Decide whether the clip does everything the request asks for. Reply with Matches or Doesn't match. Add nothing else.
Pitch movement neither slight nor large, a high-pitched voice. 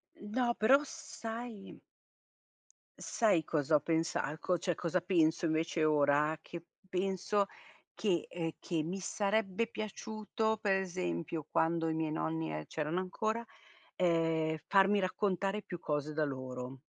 Doesn't match